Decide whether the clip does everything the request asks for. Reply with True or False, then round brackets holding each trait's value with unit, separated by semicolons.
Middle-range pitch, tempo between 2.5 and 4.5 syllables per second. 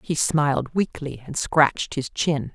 True (145 Hz; 4.1 syllables/s)